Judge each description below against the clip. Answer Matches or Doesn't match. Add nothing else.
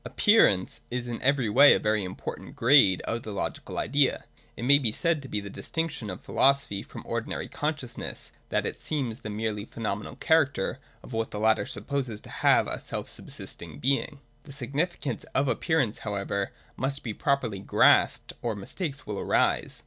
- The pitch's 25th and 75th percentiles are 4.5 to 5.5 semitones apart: Matches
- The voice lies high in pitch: Doesn't match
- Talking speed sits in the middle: Matches